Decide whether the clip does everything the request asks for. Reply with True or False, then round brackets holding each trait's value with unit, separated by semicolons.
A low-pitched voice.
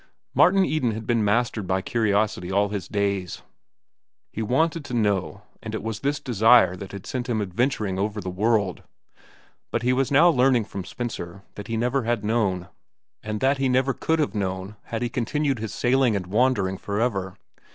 True (110 Hz)